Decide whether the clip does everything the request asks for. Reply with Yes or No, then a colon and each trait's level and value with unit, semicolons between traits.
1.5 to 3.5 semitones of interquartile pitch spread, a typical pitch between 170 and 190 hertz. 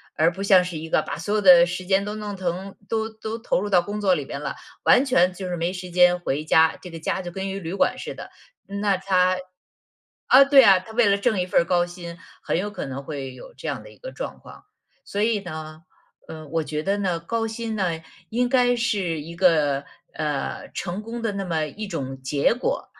No: average, 4.0 semitones; medium, 185 Hz